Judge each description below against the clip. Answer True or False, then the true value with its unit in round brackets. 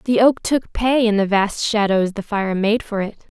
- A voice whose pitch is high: True (215 Hz)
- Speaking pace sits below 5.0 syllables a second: True (4.6 syllables/s)